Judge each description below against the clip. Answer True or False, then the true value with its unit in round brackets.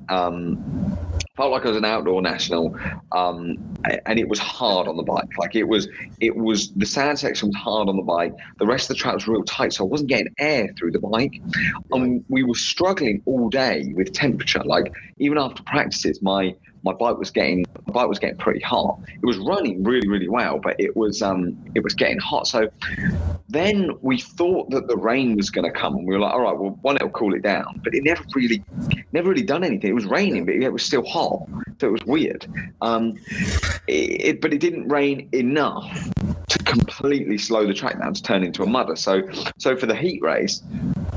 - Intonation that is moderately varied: False (6.7 semitones)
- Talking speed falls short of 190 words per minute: False (220 wpm)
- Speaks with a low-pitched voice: True (110 Hz)